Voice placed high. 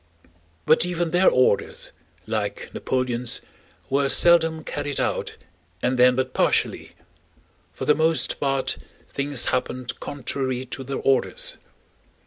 No: low, 135 Hz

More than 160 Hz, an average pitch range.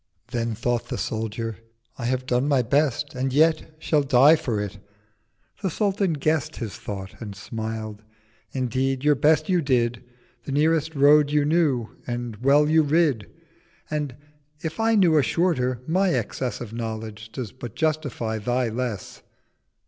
No: low, 130 Hz; average, 4.9 semitones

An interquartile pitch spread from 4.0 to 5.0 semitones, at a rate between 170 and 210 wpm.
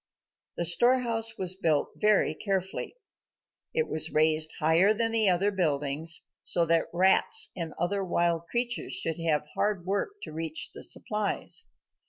No: average, 4.6 semitones; average, 145 wpm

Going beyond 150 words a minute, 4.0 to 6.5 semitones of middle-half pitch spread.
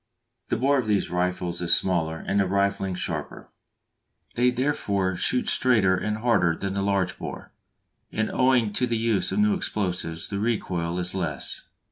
Yes: average, 165 wpm; average, 4.5 semitones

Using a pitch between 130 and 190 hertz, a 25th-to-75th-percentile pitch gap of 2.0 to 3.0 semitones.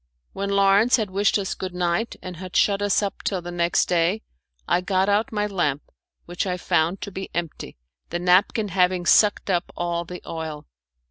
Yes: medium, 185 Hz; narrow, 2.4 semitones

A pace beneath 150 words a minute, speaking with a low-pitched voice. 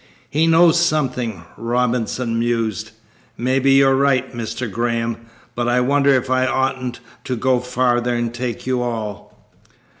Yes: average, 140 wpm; low, 125 Hz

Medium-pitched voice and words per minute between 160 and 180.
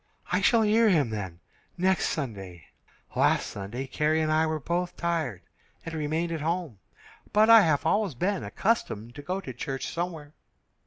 Yes: medium, 155 Hz; average, 165 wpm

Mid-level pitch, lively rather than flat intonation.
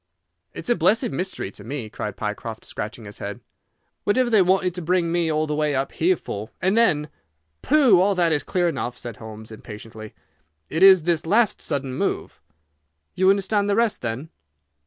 Yes: medium, 165 Hz; wide, 8.2 semitones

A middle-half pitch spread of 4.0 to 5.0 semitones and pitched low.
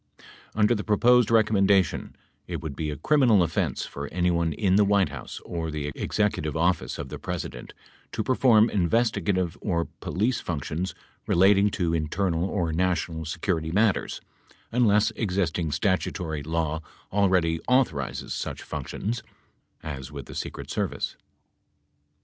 Yes: average, 4.5 semitones; very low, 90 Hz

